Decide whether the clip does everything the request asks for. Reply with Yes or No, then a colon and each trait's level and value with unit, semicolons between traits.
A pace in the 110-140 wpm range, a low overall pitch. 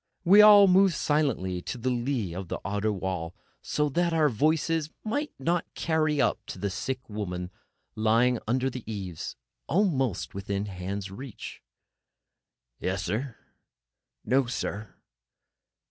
Yes: slow, 135 wpm; low, 125 Hz